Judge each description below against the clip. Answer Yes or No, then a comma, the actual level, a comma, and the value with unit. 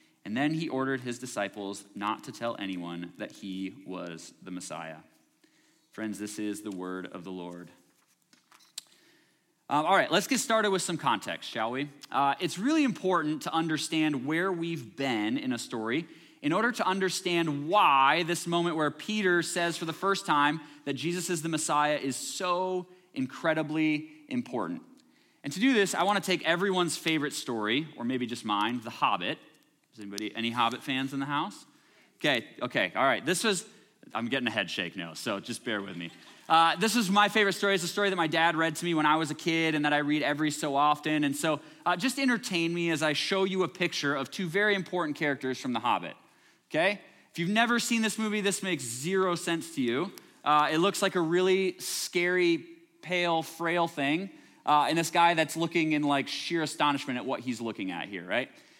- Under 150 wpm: No, average, 200 wpm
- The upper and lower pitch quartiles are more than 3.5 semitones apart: Yes, average, 5.3 semitones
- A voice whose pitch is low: No, medium, 160 Hz